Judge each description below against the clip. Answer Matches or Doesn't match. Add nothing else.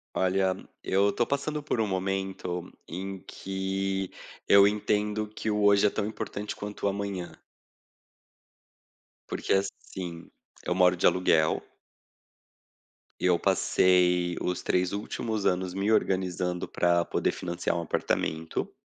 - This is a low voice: Matches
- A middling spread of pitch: Doesn't match